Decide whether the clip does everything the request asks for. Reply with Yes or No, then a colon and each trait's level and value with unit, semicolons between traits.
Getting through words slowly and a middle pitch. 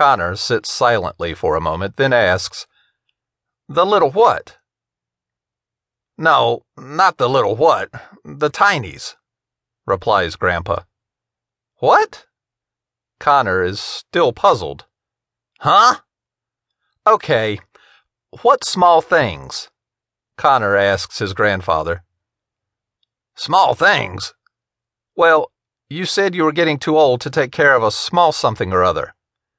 No: slow, 105 wpm; low, 125 Hz